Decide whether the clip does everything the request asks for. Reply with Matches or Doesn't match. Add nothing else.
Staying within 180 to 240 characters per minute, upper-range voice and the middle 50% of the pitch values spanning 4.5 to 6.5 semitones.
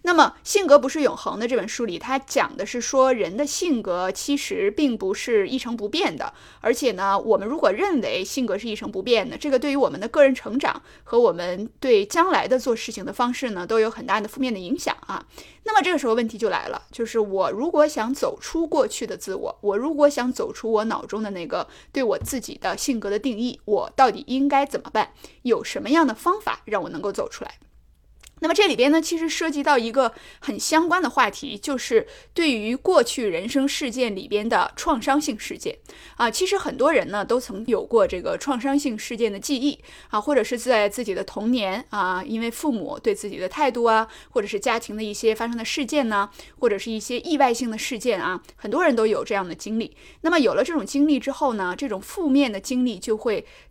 Doesn't match